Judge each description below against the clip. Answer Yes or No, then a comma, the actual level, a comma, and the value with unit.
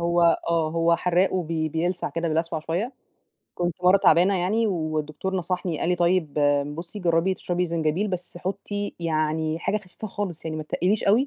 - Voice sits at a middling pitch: Yes, medium, 175 Hz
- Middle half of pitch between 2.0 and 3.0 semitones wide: Yes, narrow, 2.5 semitones